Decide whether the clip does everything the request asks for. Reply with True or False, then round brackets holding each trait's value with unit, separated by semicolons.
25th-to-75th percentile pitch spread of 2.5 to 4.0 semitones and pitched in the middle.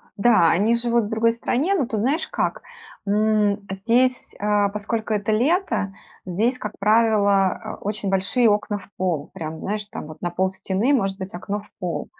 False (3.1 semitones; 210 Hz)